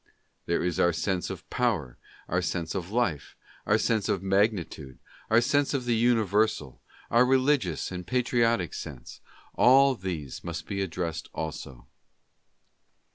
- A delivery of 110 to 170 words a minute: Yes, average, 140 wpm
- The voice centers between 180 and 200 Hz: No, very low, 95 Hz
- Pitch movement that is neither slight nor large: No, wide, 6.0 semitones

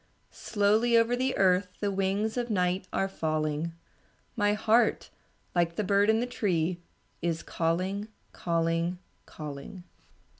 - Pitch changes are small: No, average, 4.0 semitones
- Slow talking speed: Yes, slow, 125 wpm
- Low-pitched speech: No, high, 190 Hz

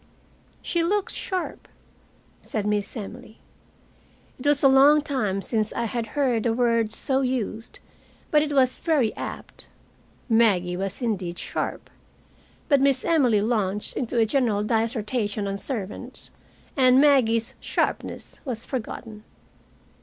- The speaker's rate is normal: No, slow, 130 wpm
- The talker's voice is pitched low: No, high, 235 Hz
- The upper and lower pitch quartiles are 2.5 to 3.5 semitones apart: No, average, 4.1 semitones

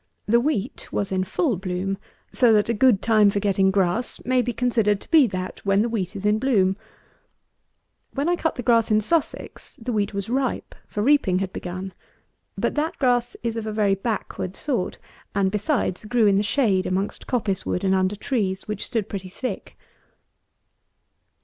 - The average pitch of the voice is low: No, high, 210 Hz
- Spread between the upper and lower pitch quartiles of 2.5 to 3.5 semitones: No, average, 4.0 semitones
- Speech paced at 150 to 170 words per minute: No, average, 185 wpm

